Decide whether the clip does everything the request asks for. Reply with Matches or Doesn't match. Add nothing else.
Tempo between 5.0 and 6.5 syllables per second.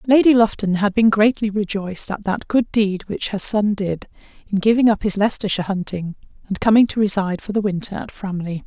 Matches